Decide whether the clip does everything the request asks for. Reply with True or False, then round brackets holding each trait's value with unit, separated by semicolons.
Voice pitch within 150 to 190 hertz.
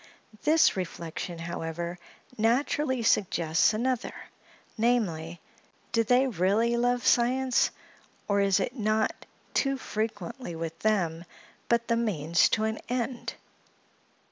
False (220 Hz)